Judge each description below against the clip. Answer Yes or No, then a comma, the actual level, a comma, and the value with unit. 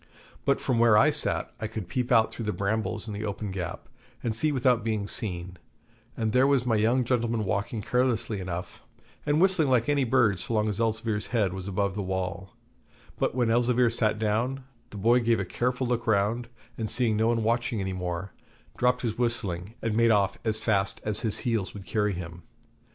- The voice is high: No, low, 110 Hz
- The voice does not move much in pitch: No, average, 3.2 semitones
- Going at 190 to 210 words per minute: Yes, average, 200 wpm